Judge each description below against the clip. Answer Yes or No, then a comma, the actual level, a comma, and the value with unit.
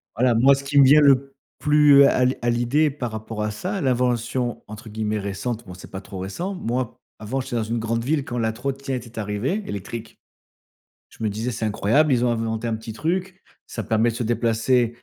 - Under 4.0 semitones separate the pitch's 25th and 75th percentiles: Yes, average, 3.5 semitones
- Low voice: Yes, low, 120 Hz